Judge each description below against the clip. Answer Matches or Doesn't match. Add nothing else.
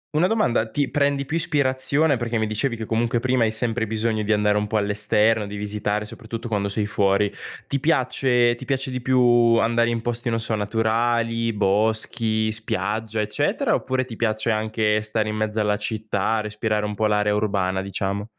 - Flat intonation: Matches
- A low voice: Matches